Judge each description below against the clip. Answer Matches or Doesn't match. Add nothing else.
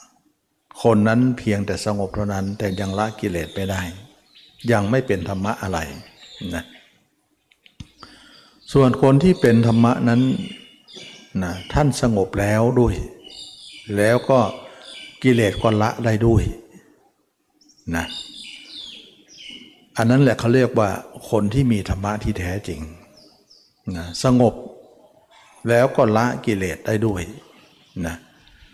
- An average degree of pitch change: Matches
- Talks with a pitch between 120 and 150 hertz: Doesn't match